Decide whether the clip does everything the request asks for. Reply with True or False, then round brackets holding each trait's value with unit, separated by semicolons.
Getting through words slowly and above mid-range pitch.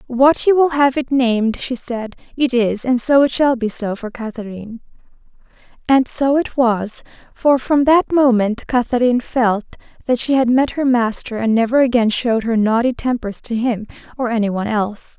False (180 wpm; 245 Hz)